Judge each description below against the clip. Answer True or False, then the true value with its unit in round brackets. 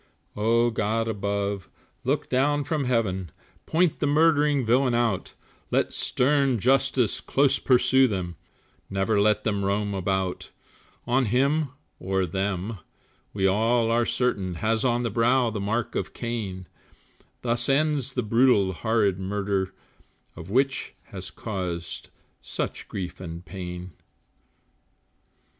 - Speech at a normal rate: False (120 wpm)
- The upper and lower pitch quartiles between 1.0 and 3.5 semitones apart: False (4.7 semitones)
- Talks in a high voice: False (115 Hz)